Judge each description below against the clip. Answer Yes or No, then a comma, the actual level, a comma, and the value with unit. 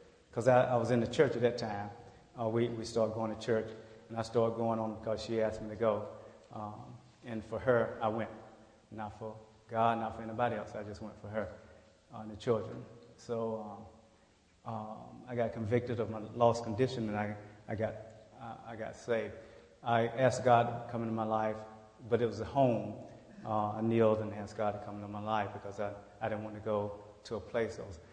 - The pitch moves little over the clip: Yes, narrow, 1.3 semitones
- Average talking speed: No, fast, 220 wpm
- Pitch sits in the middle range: No, low, 110 Hz